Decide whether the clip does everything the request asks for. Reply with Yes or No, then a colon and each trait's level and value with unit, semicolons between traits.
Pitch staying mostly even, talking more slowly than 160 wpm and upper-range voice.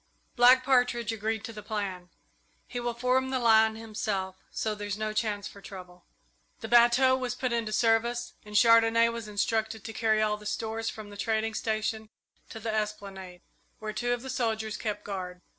No: narrow, 2.0 semitones; average, 180 wpm; high, 220 Hz